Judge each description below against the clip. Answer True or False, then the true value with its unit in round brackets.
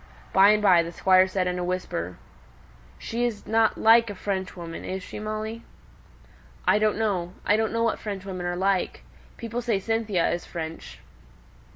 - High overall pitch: True (195 Hz)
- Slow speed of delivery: False (165 wpm)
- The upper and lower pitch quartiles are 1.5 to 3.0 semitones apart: False (3.4 semitones)